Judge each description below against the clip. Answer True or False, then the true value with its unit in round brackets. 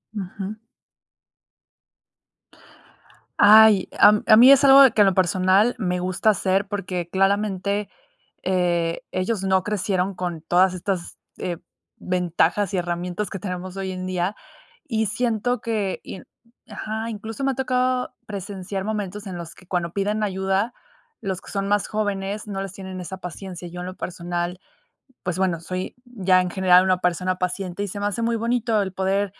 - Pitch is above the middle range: True (195 Hz)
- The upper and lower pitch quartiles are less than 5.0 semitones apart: True (2.4 semitones)